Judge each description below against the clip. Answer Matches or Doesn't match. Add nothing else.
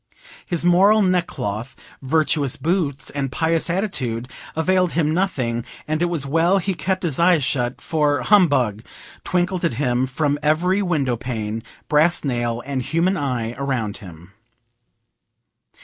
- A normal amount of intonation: Doesn't match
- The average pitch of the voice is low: Doesn't match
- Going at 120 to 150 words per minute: Matches